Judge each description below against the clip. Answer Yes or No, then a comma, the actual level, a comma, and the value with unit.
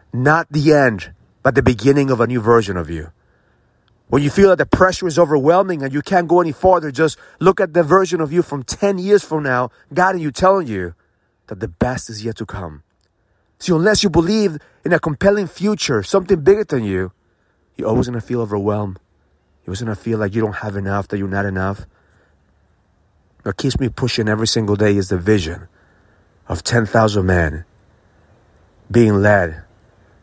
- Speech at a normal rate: Yes, average, 195 wpm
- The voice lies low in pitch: Yes, low, 115 Hz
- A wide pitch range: Yes, wide, 8.3 semitones